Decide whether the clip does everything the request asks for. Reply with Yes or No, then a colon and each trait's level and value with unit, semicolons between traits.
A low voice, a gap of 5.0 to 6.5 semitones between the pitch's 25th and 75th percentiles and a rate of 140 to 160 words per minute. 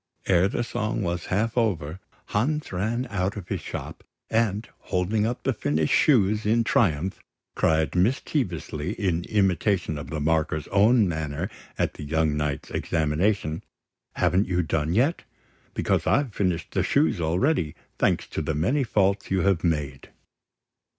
Yes: very low, 95 Hz; average, 5.3 semitones; average, 150 wpm